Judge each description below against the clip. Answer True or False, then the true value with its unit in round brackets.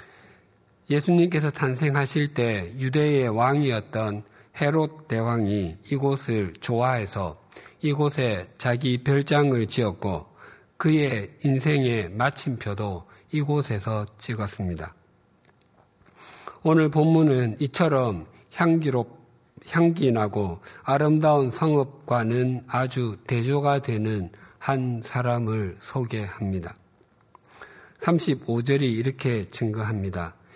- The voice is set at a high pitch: False (125 Hz)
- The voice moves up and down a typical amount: True (5.0 semitones)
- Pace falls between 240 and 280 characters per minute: False (210 characters per minute)